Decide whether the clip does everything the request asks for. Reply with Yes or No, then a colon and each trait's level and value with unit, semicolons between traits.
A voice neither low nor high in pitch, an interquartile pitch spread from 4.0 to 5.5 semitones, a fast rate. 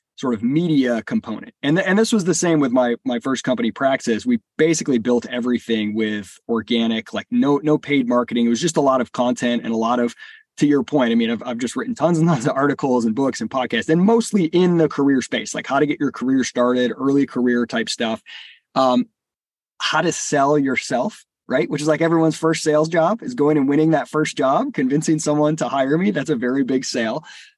Yes: medium, 145 Hz; average, 4.7 semitones; fast, 225 wpm